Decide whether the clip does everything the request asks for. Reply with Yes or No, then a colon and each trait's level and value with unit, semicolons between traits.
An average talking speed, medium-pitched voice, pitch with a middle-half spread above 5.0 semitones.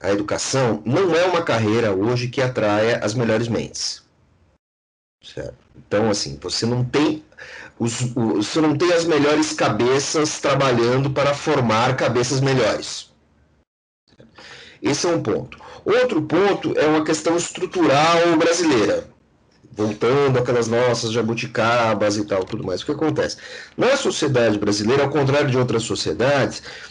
No: average, 140 wpm; low, 125 Hz; wide, 5.4 semitones